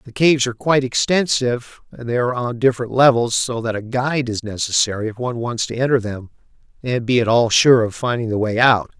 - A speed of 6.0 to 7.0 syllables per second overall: Yes, 6.2 syllables/s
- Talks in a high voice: No, low, 120 Hz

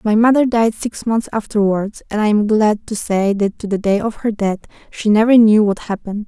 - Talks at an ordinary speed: No, fast, 230 wpm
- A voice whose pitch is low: No, high, 215 Hz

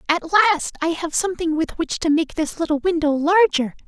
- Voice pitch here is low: No, very high, 300 Hz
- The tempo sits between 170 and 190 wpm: No, average, 200 wpm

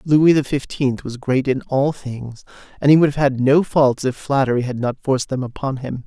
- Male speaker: Yes, male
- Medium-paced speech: No, fast, 230 wpm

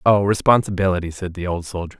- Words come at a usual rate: Yes, average, 150 wpm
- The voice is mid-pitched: No, very low, 95 Hz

